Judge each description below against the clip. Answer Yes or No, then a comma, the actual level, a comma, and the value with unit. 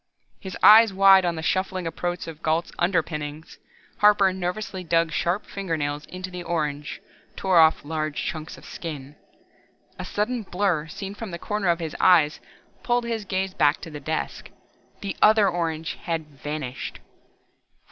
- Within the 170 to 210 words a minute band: No, average, 155 wpm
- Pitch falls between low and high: Yes, medium, 175 Hz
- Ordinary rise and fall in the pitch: Yes, average, 3.5 semitones